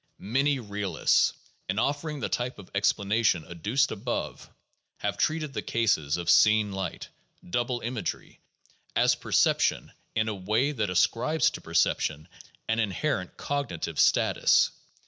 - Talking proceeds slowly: Yes, slow, 130 wpm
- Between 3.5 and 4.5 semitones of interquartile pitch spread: No, average, 5.2 semitones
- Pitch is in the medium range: No, low, 110 Hz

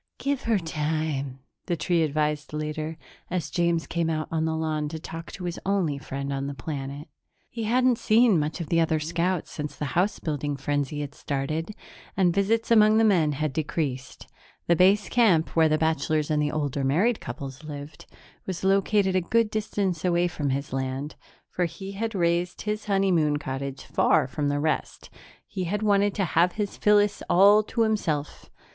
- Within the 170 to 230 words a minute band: Yes, average, 180 wpm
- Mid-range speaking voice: Yes, medium, 160 Hz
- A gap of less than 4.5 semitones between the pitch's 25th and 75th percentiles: No, average, 4.8 semitones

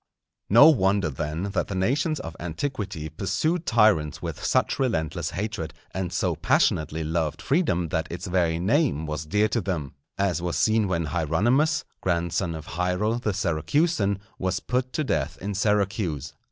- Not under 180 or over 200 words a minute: No, average, 155 wpm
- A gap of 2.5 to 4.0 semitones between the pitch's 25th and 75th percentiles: No, average, 5.3 semitones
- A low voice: Yes, very low, 95 Hz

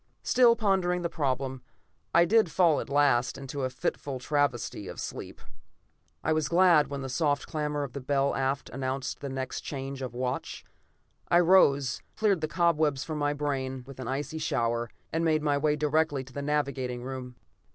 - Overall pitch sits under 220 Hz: Yes, medium, 140 Hz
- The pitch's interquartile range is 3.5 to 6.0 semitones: No, average, 3.0 semitones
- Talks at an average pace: Yes, average, 180 wpm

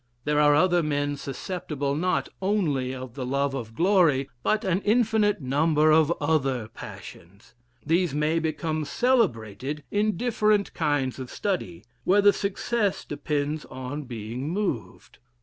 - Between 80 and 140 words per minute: Yes, slow, 135 wpm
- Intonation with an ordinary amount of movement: No, wide, 5.7 semitones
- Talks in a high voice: No, medium, 150 Hz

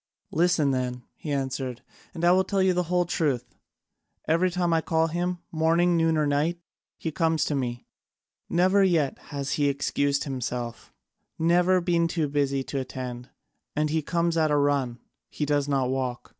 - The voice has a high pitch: No, medium, 155 Hz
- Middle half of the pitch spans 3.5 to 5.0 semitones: Yes, average, 4.0 semitones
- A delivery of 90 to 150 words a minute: No, average, 170 wpm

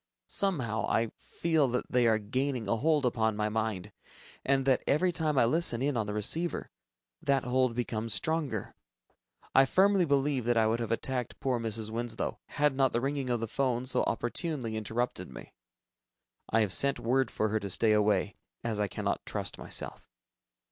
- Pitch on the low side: Yes, low, 120 Hz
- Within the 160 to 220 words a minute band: Yes, average, 180 wpm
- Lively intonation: No, average, 3.8 semitones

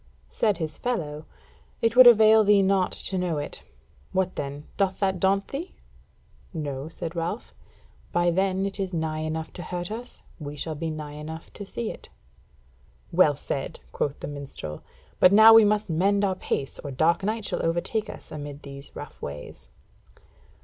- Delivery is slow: No, average, 170 wpm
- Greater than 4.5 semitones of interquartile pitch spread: Yes, average, 4.9 semitones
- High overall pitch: No, medium, 175 Hz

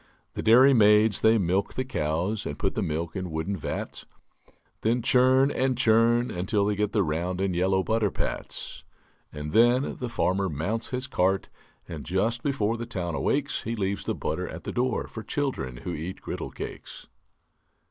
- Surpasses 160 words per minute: Yes, average, 180 wpm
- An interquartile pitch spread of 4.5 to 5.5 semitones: Yes, average, 4.8 semitones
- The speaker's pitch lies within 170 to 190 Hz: No, low, 105 Hz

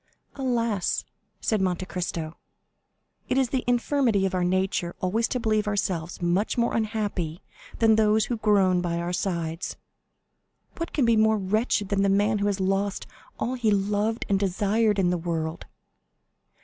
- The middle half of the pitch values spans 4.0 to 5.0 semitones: No, average, 3.4 semitones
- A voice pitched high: Yes, high, 200 Hz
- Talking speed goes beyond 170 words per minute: No, average, 160 wpm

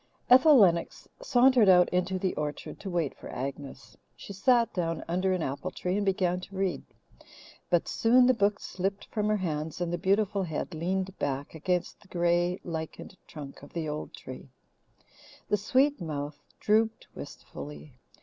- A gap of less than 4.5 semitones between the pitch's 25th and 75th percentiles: Yes, average, 4.1 semitones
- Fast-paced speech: No, average, 165 wpm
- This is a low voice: No, medium, 180 Hz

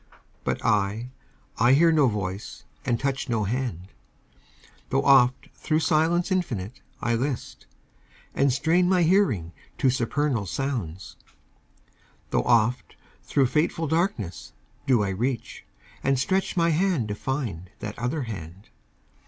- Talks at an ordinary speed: No, slow, 130 wpm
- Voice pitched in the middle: No, low, 130 Hz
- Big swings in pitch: Yes, wide, 6.1 semitones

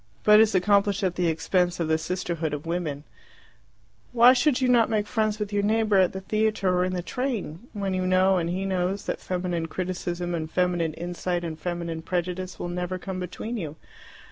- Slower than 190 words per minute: No, average, 195 wpm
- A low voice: No, medium, 185 Hz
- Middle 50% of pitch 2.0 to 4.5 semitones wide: Yes, average, 2.9 semitones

